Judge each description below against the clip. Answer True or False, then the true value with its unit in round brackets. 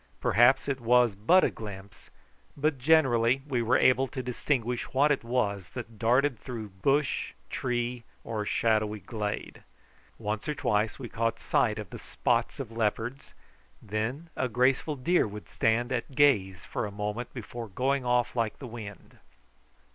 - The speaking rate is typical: True (155 wpm)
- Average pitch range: True (3.4 semitones)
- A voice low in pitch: True (120 Hz)